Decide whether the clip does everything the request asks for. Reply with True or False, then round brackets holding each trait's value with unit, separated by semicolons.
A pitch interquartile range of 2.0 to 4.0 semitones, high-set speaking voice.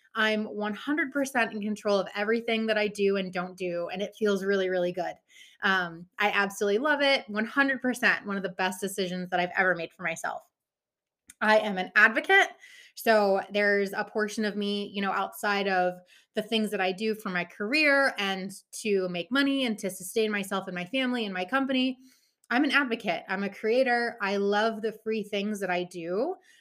True (3.1 semitones; 205 Hz)